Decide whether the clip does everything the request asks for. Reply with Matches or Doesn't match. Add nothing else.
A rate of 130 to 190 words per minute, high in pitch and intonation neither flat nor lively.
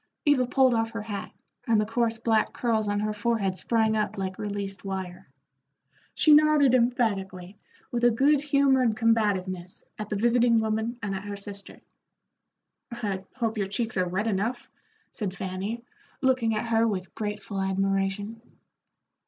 Matches